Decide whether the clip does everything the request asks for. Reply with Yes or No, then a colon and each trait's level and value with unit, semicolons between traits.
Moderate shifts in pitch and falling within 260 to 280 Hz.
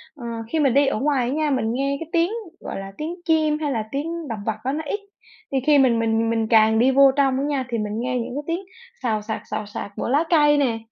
Yes: average, 4.6 semitones; very high, 265 Hz